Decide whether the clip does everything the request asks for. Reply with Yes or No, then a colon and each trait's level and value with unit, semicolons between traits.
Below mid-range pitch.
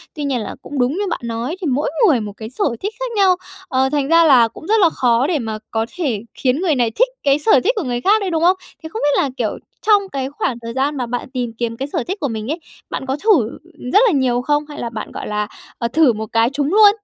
No: very high, 275 Hz